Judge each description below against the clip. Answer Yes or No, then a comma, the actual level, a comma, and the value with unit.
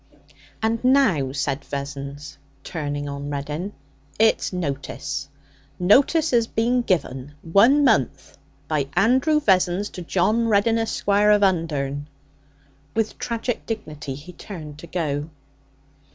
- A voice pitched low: No, medium, 180 Hz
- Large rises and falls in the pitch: Yes, wide, 7.7 semitones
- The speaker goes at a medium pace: No, slow, 115 wpm